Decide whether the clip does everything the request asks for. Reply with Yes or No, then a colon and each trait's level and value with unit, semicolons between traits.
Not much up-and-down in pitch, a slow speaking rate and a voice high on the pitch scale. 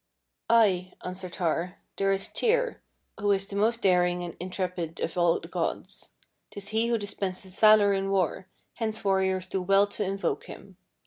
No: narrow, 2.1 semitones; average, 170 wpm; high, 195 Hz